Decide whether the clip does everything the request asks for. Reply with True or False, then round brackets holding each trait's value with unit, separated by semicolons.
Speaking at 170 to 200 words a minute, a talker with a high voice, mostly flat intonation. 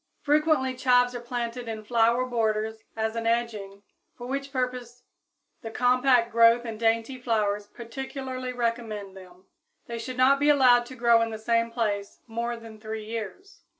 False (160 wpm; 235 Hz; 2.2 semitones)